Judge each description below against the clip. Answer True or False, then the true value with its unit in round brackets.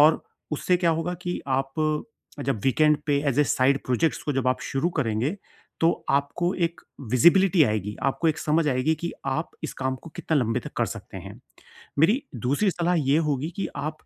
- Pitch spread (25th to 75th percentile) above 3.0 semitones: True (4.0 semitones)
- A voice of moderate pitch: True (150 Hz)